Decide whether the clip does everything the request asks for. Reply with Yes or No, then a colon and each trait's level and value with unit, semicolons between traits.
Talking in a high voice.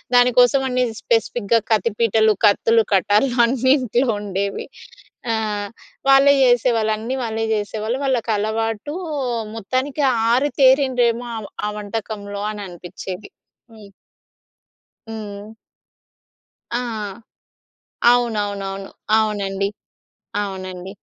Yes: high, 220 Hz